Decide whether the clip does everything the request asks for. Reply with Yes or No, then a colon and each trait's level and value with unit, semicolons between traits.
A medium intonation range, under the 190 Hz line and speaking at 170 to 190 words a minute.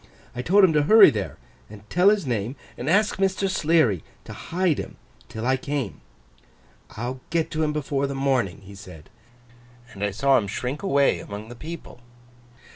No: wide, 7.0 semitones; low, 135 Hz; average, 180 wpm